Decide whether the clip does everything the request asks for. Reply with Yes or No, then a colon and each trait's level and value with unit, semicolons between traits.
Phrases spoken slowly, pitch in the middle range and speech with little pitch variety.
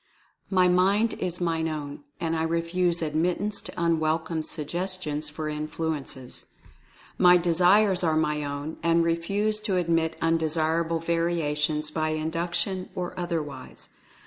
Yes: slow, 125 wpm; medium, 165 Hz; narrow, 2.2 semitones